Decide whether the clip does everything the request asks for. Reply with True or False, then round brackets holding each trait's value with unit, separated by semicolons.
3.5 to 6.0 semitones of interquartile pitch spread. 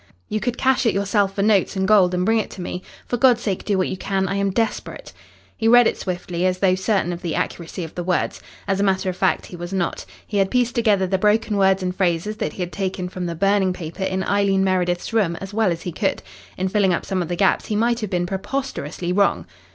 False (2.5 semitones)